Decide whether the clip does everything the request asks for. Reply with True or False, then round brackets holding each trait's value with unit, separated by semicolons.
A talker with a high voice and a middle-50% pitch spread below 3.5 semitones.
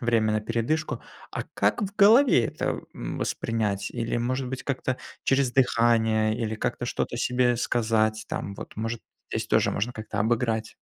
False (115 Hz; 2.4 semitones)